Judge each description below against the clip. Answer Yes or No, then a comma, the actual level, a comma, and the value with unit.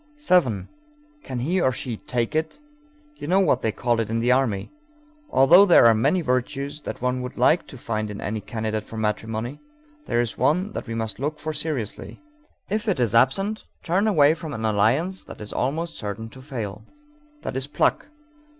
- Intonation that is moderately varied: No, wide, 5.8 semitones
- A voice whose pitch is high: No, low, 125 Hz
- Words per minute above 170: Yes, average, 190 wpm